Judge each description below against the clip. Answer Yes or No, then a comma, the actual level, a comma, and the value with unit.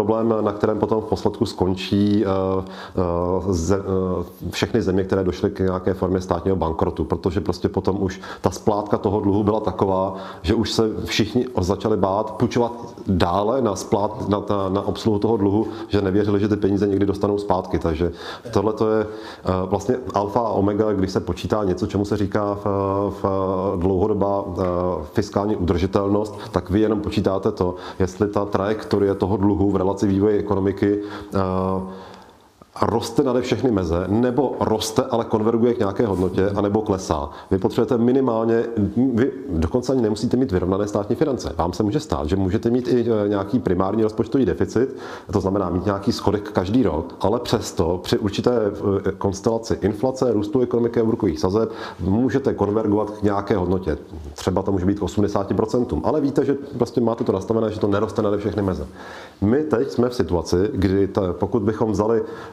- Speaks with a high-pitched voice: No, low, 100 Hz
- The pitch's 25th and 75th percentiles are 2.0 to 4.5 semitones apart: Yes, average, 2.7 semitones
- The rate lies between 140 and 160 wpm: No, fast, 170 wpm